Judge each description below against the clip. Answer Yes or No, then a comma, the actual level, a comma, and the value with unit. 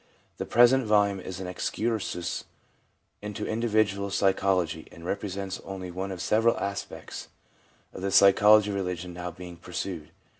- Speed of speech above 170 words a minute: No, average, 140 wpm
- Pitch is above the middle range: No, very low, 95 Hz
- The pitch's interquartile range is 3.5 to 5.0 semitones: No, narrow, 2.4 semitones